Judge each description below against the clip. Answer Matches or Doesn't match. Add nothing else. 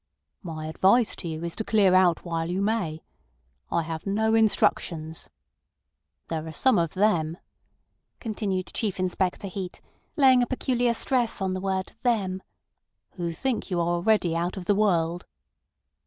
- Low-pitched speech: Doesn't match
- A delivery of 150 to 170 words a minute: Matches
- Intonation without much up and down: Doesn't match